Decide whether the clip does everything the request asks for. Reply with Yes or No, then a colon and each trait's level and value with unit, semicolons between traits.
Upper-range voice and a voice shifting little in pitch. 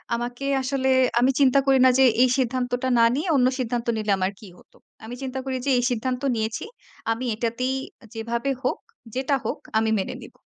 Yes: very high, 250 Hz; narrow, 2.2 semitones